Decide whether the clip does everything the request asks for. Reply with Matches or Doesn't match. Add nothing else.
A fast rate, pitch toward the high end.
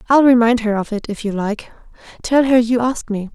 Matches